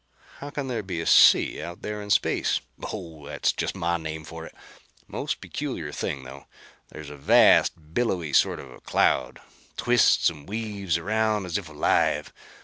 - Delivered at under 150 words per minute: No, average, 170 wpm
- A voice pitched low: Yes, very low, 85 Hz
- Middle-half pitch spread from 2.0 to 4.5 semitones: No, wide, 5.5 semitones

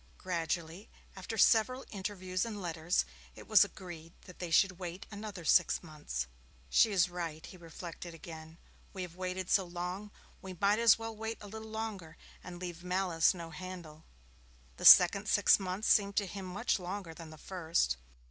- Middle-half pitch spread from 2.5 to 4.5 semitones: Yes, average, 3.2 semitones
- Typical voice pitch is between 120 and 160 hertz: No, medium, 185 Hz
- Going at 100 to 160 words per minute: No, average, 170 wpm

